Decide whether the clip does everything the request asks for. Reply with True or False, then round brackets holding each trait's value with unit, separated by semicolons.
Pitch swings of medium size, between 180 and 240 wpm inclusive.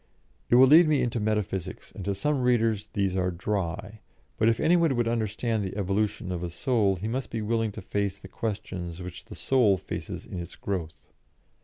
True (3.6 semitones; 200 wpm)